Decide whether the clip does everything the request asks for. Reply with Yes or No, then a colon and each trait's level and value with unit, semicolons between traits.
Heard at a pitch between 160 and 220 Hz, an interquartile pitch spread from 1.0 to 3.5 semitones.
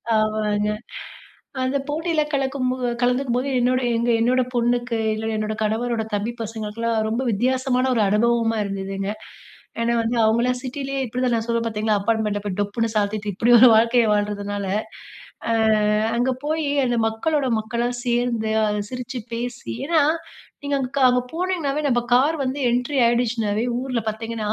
No: high, 235 Hz; average, 2.8 semitones